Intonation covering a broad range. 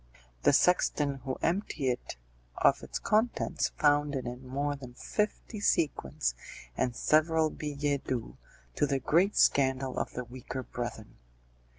No: average, 3.4 semitones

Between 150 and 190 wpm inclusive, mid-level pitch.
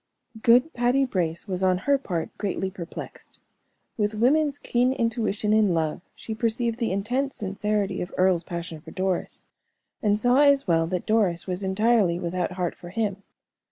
No: average, 160 wpm; high, 205 Hz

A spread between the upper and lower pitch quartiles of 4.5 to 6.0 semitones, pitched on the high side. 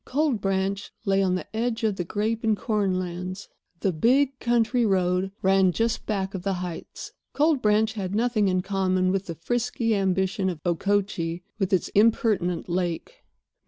No: average, 3.3 semitones; high, 195 Hz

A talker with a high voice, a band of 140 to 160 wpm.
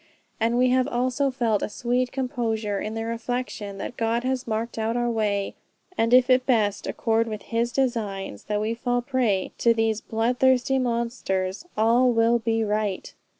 No: high, 230 Hz; average, 180 wpm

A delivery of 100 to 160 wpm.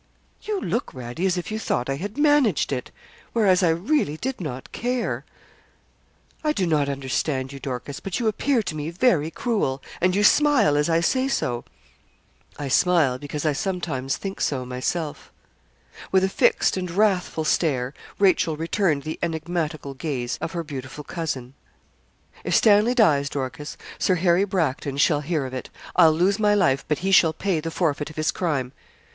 No: average, 175 wpm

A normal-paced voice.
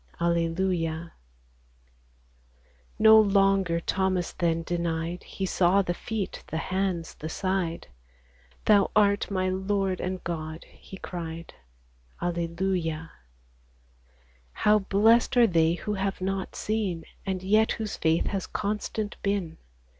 No: slow, 115 wpm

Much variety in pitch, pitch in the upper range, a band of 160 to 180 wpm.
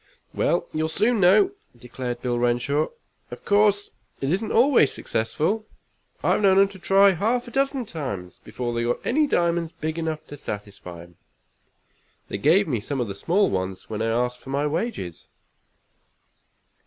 No: wide, 8.9 semitones; medium, 155 Hz; average, 165 wpm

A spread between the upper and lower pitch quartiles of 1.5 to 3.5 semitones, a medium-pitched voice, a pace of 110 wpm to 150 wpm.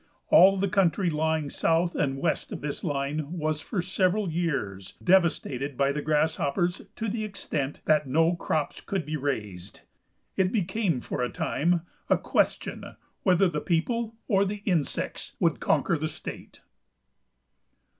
No: average, 4.6 semitones; medium, 165 Hz; average, 145 wpm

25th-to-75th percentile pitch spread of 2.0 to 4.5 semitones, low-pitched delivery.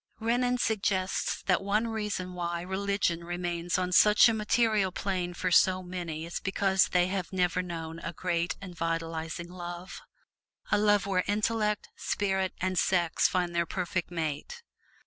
No: narrow, 2.6 semitones; medium, 185 Hz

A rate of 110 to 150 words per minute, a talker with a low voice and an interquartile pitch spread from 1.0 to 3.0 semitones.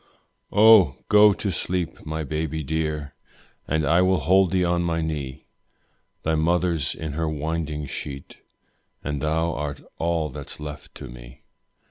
Yes: average, 145 wpm; very low, 80 Hz; narrow, 2.6 semitones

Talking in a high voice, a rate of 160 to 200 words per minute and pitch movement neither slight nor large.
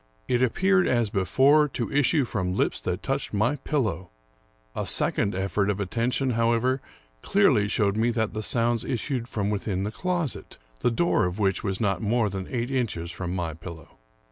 No: low, 115 Hz; average, 175 wpm; average, 4.6 semitones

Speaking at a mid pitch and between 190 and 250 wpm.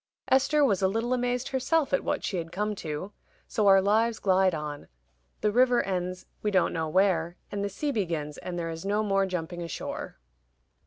No: high, 195 Hz; average, 195 wpm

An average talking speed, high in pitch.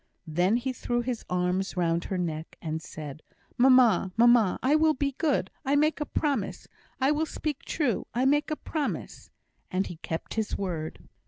Yes: average, 175 wpm; high, 240 Hz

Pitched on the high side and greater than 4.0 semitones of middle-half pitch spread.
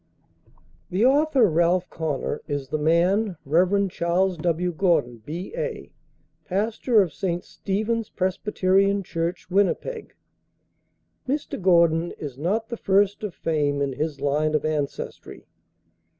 No: medium, 180 Hz; average, 4.4 semitones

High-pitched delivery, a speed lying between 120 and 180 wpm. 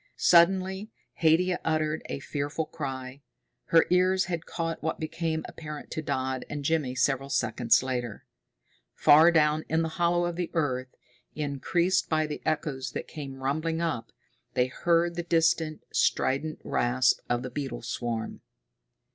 No: medium, 155 Hz; average, 145 wpm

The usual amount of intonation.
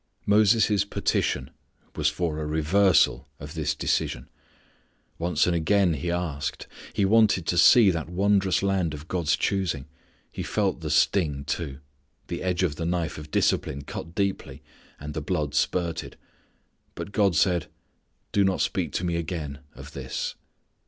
Yes: average, 4.1 semitones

